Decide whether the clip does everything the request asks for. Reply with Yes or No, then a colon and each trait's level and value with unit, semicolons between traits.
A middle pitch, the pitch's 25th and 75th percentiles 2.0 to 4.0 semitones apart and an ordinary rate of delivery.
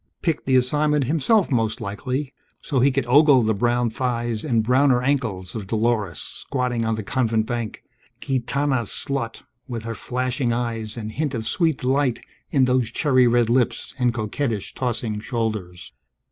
No: low, 120 Hz; average, 2.9 semitones; average, 160 wpm